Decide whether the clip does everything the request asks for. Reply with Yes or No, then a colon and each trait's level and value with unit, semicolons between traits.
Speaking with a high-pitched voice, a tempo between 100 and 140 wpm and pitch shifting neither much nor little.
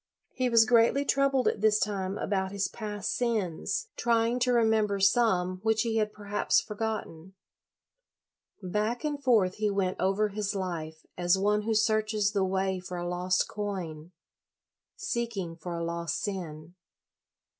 No: high, 205 Hz; average, 155 wpm; average, 3.2 semitones